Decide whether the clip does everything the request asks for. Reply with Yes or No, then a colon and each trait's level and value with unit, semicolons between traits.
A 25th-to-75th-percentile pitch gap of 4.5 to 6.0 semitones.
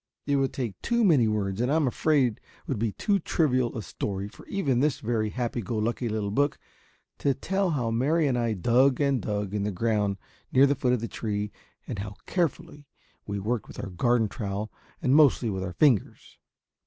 Yes: average, 4.9 semitones